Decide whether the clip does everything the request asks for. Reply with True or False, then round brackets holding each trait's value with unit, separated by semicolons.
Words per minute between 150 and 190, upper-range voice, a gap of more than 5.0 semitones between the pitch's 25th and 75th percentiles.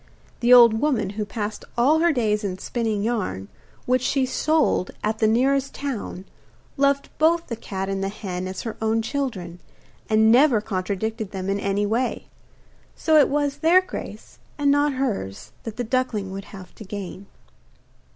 True (170 wpm; 220 Hz; 5.5 semitones)